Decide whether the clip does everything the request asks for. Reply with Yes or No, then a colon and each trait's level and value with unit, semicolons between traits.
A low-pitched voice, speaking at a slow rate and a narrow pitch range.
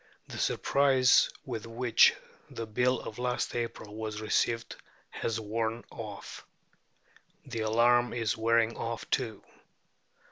Yes: low, 115 Hz; slow, 115 wpm; narrow, 1.7 semitones